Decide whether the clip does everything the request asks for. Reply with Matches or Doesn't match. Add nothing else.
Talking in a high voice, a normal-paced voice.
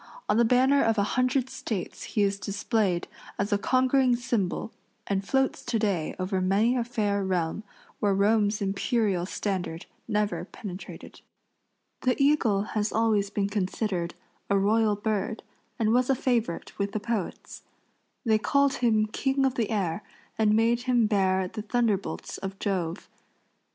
Matches